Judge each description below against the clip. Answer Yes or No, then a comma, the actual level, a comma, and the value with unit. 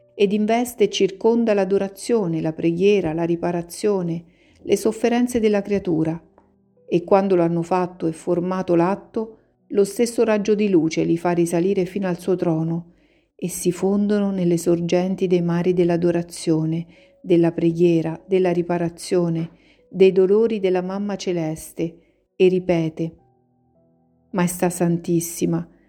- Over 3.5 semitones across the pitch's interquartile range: No, average, 2.7 semitones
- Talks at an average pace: Yes, average, 125 wpm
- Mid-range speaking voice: Yes, medium, 175 Hz